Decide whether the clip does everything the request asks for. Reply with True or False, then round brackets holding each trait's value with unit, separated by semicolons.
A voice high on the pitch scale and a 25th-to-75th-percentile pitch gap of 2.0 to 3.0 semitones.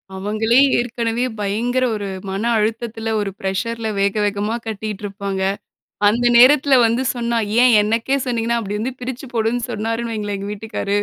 True (225 Hz; 2.4 semitones)